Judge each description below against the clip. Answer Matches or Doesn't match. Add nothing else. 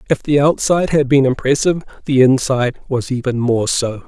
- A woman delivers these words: Doesn't match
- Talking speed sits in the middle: Matches